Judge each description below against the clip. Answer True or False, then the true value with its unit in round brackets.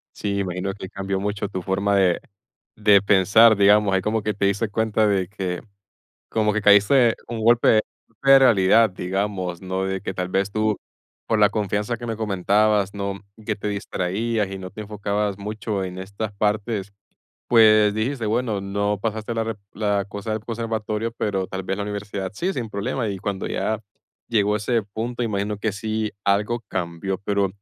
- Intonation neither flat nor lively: False (1.9 semitones)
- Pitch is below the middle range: True (105 Hz)